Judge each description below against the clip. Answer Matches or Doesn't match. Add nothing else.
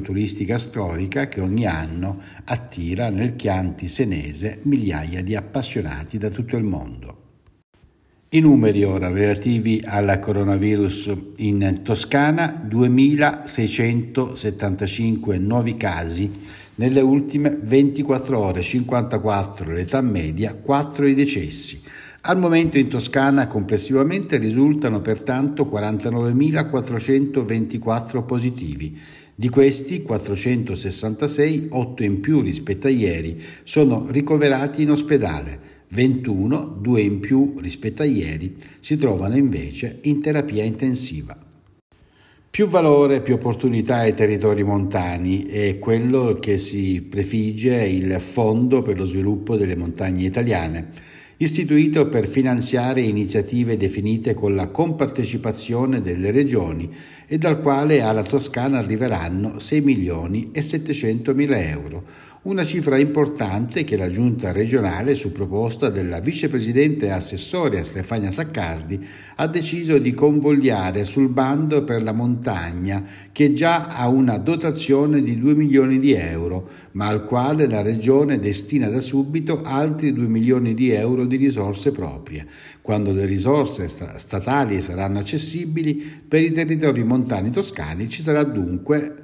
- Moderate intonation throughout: Doesn't match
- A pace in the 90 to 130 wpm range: Matches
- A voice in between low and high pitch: Doesn't match